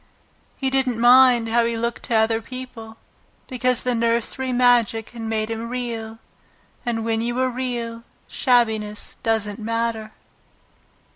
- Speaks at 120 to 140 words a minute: Yes, slow, 135 wpm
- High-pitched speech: Yes, high, 230 Hz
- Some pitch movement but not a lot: No, narrow, 1.7 semitones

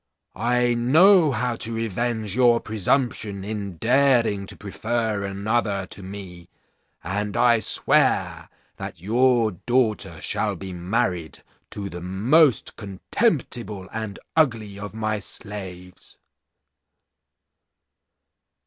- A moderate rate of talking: No, slow, 105 wpm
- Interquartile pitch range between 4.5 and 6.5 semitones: No, average, 3.5 semitones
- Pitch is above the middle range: No, low, 110 Hz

